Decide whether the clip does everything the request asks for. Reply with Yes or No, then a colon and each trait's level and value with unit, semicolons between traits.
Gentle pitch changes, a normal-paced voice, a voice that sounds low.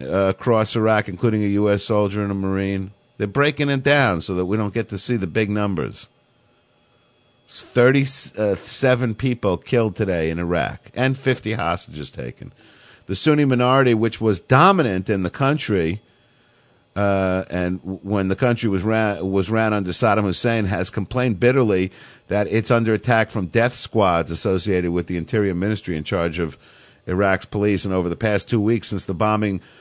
No: average, 3.8 semitones; average, 170 wpm; low, 105 Hz